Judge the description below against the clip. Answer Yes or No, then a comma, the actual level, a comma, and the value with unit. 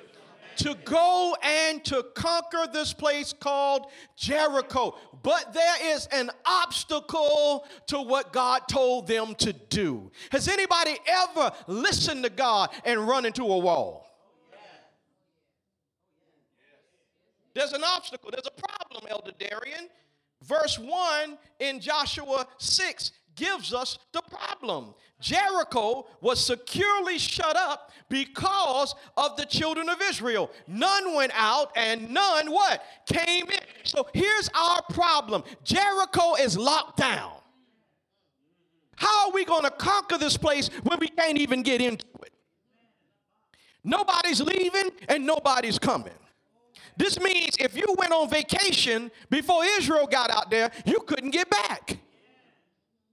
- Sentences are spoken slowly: Yes, slow, 125 wpm